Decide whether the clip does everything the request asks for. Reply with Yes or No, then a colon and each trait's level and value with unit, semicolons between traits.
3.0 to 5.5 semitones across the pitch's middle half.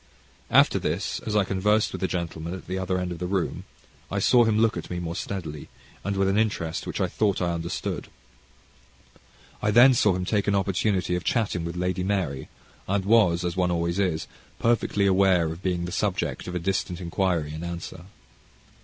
No: narrow, 2.6 semitones